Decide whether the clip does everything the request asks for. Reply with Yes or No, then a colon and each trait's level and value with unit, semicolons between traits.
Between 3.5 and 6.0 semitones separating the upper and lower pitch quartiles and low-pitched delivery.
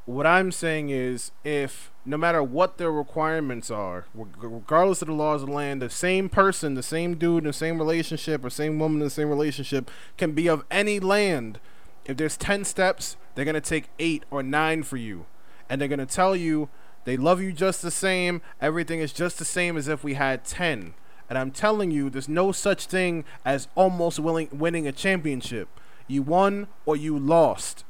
No: average, 4.0 semitones; medium, 155 Hz